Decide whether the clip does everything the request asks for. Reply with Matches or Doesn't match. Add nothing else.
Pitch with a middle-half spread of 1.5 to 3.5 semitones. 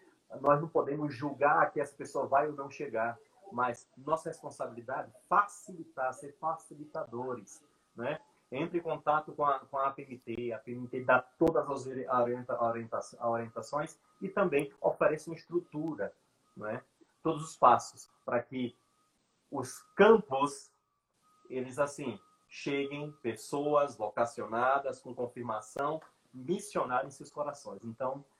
Doesn't match